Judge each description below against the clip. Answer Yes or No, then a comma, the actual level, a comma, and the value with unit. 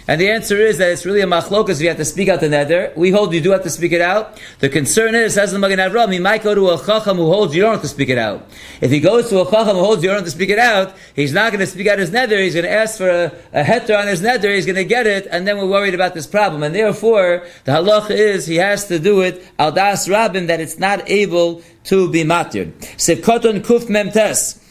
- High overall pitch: Yes, high, 195 Hz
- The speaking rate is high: Yes, fast, 280 wpm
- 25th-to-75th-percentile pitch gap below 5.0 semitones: Yes, average, 3.4 semitones